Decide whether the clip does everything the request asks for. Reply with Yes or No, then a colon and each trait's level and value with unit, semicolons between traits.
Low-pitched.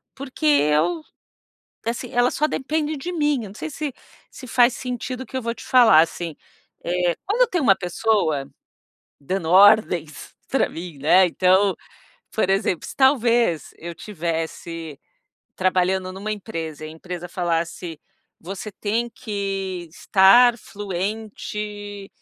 No: high, 195 Hz